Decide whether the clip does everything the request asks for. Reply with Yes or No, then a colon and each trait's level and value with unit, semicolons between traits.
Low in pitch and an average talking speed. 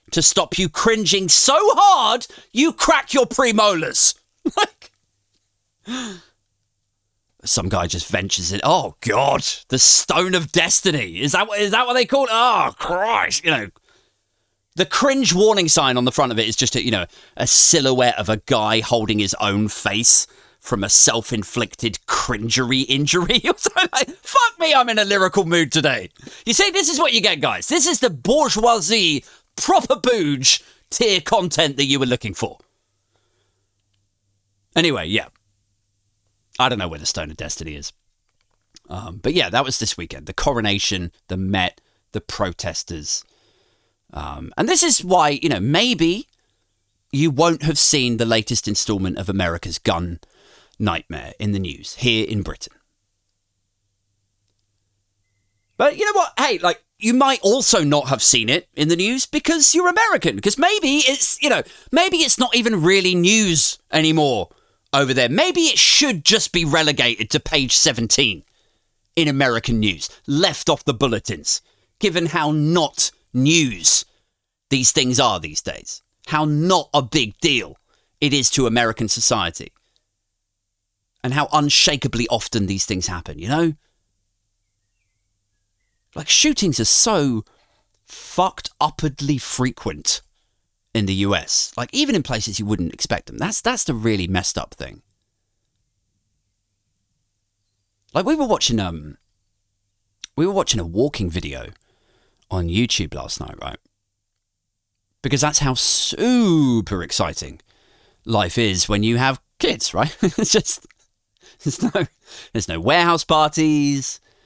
Yes: low, 120 Hz; average, 145 wpm